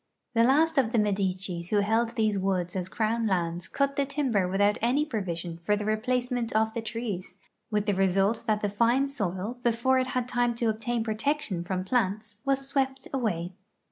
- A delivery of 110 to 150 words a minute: No, average, 185 wpm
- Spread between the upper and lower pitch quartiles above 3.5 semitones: Yes, average, 4.2 semitones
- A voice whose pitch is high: Yes, high, 220 Hz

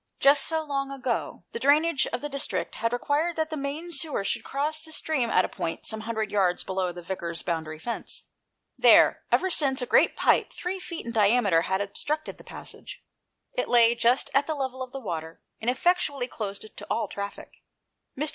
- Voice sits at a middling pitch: No, very high, 255 Hz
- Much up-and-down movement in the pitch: Yes, wide, 6.8 semitones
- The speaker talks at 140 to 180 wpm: No, average, 200 wpm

